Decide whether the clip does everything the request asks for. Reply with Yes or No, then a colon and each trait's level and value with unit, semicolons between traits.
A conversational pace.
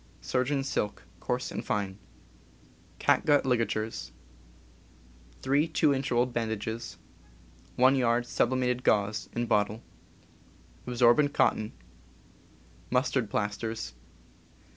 No: slow, 90 wpm